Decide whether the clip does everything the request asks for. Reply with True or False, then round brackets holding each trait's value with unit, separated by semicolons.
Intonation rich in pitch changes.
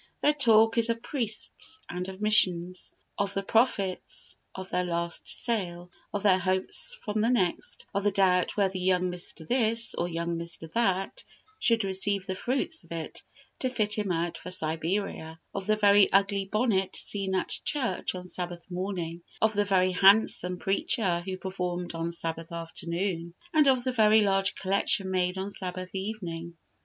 False (3.0 semitones)